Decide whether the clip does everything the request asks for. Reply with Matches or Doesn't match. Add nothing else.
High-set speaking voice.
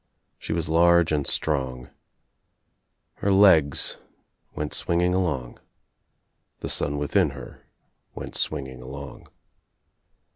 Doesn't match